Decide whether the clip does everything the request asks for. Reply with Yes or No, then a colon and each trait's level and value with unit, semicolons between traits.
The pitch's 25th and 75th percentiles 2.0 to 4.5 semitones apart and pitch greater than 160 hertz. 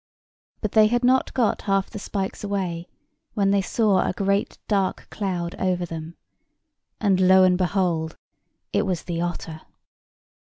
Yes: narrow, 2.4 semitones; high, 190 Hz